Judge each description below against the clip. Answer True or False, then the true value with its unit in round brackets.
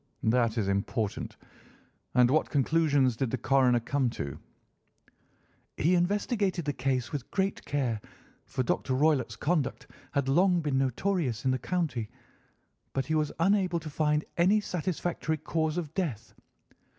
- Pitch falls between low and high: True (145 Hz)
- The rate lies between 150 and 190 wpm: False (140 wpm)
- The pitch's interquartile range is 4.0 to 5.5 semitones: True (5.1 semitones)